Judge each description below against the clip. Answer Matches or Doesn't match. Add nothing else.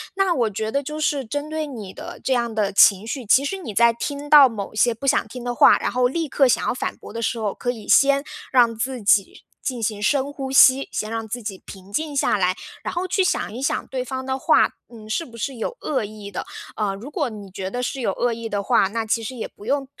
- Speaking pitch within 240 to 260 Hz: Matches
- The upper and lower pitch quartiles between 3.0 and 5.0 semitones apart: Matches